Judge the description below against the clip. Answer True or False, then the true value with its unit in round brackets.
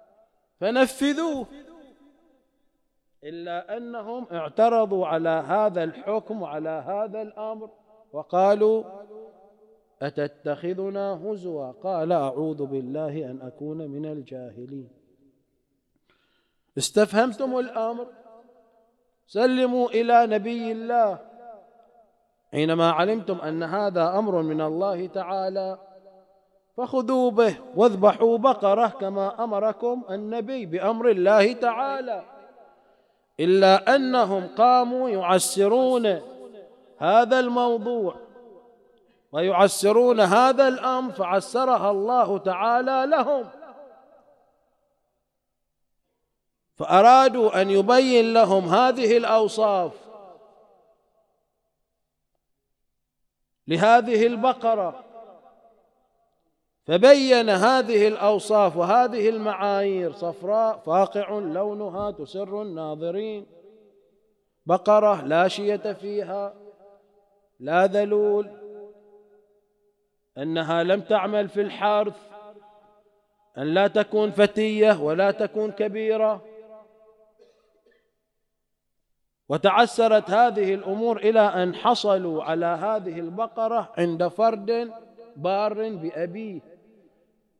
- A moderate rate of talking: False (75 wpm)